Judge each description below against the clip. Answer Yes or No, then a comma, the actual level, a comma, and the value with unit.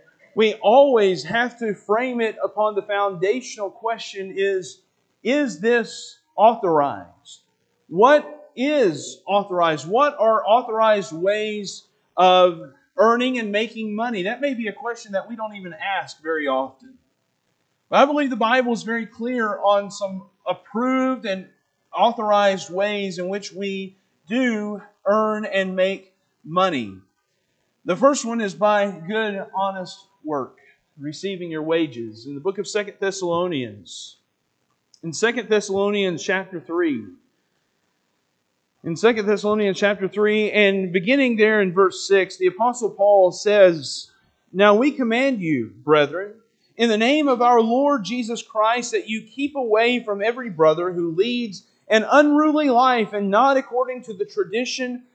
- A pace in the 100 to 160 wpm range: Yes, average, 140 wpm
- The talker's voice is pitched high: Yes, high, 210 Hz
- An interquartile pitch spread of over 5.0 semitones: No, average, 3.8 semitones